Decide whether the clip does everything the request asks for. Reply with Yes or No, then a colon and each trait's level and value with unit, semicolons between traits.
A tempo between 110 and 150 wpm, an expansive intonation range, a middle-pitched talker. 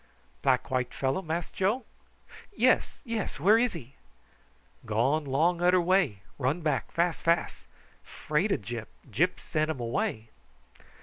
Yes: slow, 135 wpm; wide, 6.0 semitones; medium, 155 Hz